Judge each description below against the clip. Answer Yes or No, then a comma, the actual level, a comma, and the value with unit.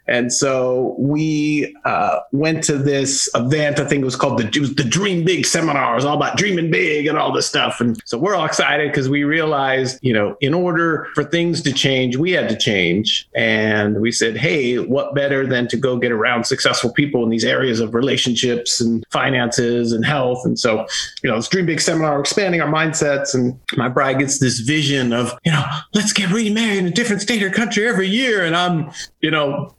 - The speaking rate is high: Yes, fast, 215 wpm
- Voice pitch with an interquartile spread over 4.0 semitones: Yes, average, 4.7 semitones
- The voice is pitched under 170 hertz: Yes, medium, 140 Hz